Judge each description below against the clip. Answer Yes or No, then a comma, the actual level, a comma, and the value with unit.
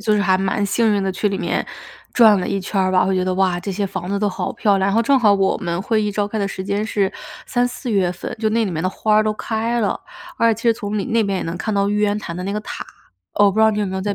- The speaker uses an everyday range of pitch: No, narrow, 2.2 semitones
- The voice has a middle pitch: No, high, 205 Hz